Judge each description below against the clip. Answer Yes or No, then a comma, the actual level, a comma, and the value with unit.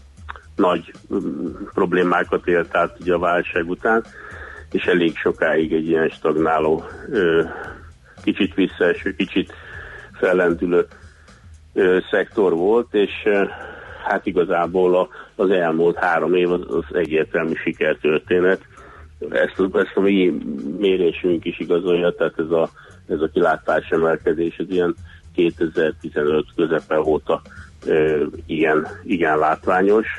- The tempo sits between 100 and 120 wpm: Yes, slow, 105 wpm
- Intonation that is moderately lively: No, narrow, 2.2 semitones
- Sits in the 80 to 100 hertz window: Yes, very low, 85 Hz